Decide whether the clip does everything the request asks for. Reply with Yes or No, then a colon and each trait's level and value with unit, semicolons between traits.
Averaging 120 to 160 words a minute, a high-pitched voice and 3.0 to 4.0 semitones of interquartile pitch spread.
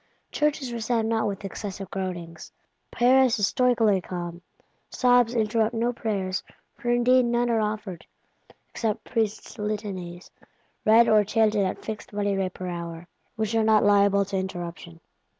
Yes: average, 145 wpm; high, 210 Hz; average, 3.4 semitones